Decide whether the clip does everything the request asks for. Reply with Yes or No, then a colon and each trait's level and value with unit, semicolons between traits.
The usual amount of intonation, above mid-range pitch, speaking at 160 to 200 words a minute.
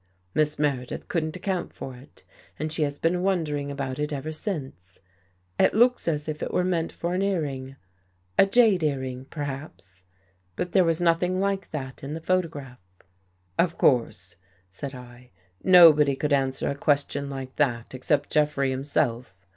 No: average, 4.1 semitones; medium, 145 Hz; average, 170 wpm